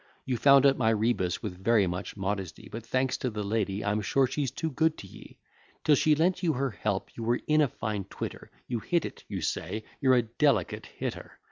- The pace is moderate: No, fast, 220 wpm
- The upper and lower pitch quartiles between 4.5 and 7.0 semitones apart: Yes, average, 5.0 semitones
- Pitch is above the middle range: No, low, 115 Hz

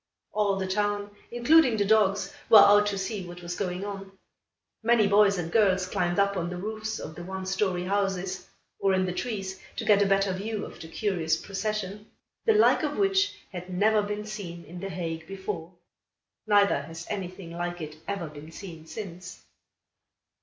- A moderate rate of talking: Yes, average, 180 wpm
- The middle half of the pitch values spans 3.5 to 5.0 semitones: No, average, 2.7 semitones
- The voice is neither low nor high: No, high, 195 Hz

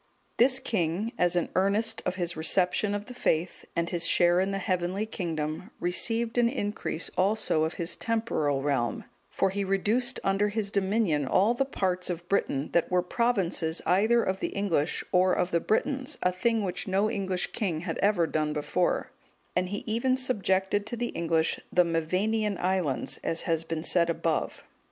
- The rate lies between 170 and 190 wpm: Yes, average, 175 wpm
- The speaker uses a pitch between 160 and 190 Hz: Yes, medium, 185 Hz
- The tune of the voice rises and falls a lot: No, average, 4.1 semitones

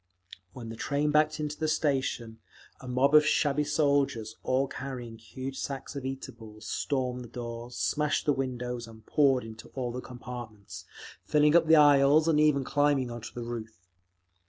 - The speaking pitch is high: No, low, 130 Hz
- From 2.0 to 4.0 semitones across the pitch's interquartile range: Yes, average, 3.6 semitones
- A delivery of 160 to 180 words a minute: Yes, average, 165 wpm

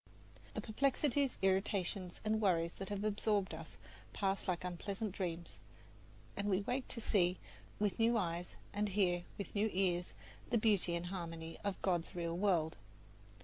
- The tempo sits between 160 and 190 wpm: No, average, 150 wpm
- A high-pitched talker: Yes, high, 195 Hz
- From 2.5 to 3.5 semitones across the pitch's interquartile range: Yes, average, 3.1 semitones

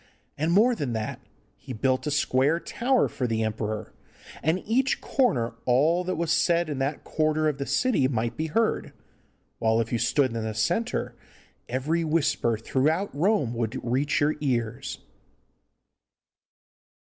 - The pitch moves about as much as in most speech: No, wide, 6.2 semitones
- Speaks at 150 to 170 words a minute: Yes, average, 155 wpm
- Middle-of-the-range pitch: Yes, medium, 145 Hz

